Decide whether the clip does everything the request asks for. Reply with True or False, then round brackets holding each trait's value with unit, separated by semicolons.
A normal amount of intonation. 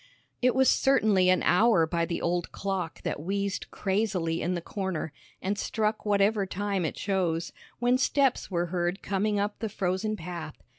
True (3.4 semitones)